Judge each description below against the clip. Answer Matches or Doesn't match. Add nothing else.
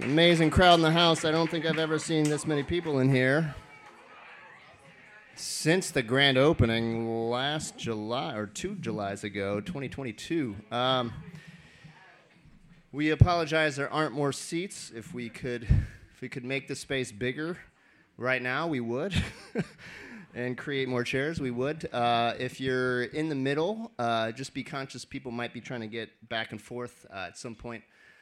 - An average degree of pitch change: Matches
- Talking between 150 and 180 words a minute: Matches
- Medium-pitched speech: Doesn't match